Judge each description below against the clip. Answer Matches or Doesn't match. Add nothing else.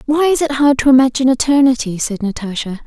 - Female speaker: Matches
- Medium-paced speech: Matches